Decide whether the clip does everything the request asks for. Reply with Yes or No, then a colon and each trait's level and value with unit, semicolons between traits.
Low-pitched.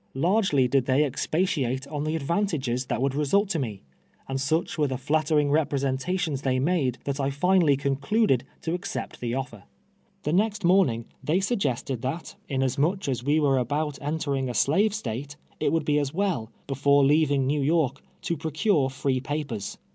No: medium, 145 Hz